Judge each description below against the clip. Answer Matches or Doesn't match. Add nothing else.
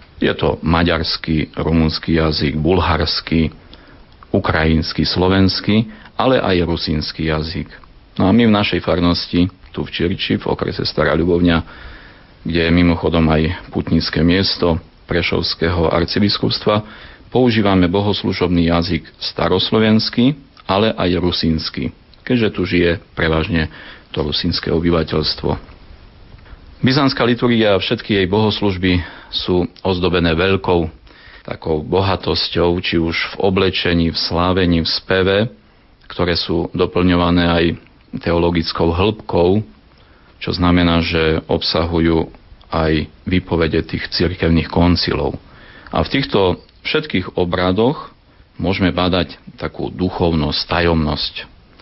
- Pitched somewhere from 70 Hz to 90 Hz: Matches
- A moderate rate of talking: Doesn't match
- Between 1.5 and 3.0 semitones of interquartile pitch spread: Matches